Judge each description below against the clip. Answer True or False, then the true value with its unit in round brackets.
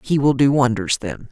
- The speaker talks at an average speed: False (230 wpm)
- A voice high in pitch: False (135 Hz)